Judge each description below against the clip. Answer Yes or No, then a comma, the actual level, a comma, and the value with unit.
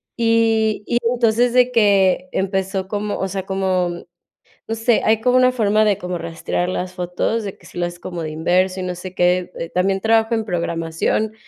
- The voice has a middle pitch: No, high, 195 Hz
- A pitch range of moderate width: Yes, average, 3.6 semitones